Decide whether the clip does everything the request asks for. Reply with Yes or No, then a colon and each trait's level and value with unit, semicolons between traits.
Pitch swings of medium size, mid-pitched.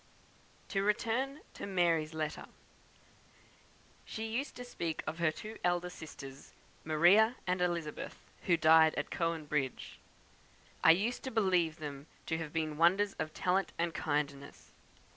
Yes: average, 3.9 semitones; medium, 170 Hz